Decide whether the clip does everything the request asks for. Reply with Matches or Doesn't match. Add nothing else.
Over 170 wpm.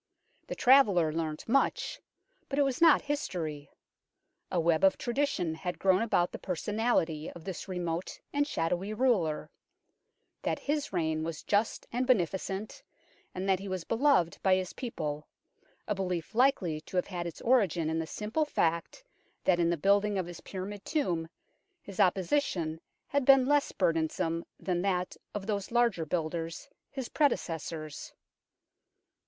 Doesn't match